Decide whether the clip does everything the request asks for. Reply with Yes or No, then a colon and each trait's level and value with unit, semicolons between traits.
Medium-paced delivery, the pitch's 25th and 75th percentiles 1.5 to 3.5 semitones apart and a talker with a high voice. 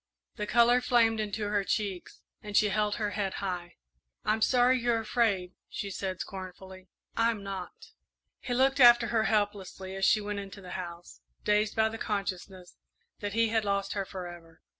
Yes: average, 170 wpm; average, 2.8 semitones; high, 205 Hz